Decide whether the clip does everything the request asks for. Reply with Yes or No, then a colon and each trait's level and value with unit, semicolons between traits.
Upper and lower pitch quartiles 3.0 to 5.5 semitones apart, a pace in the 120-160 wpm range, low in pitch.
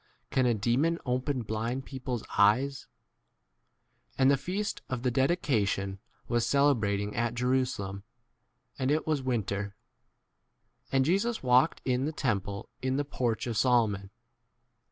Yes: average, 3.9 semitones; average, 150 wpm; low, 125 Hz